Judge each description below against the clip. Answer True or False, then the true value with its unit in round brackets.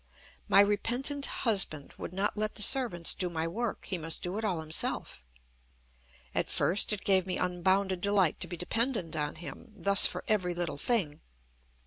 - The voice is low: False (190 Hz)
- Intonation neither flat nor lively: True (3.5 semitones)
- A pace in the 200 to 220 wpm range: False (170 wpm)